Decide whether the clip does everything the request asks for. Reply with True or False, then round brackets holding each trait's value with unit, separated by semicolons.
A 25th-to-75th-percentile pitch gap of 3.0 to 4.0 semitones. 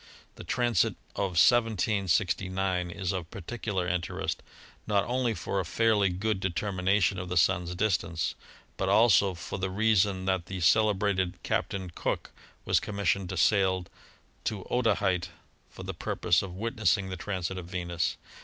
False (2.5 semitones)